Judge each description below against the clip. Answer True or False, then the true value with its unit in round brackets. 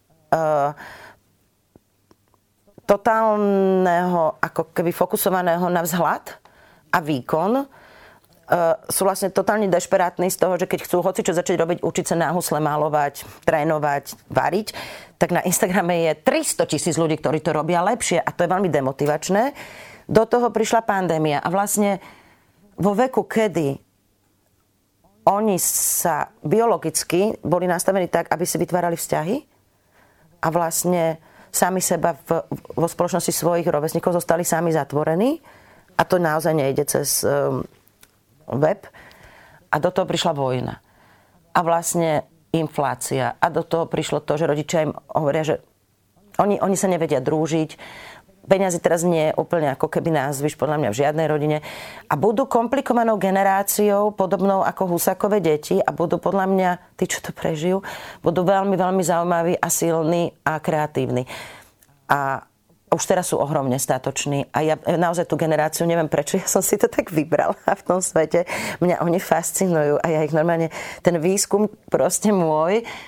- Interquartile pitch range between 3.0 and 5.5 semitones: True (3.5 semitones)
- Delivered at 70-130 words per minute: False (145 wpm)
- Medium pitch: True (170 Hz)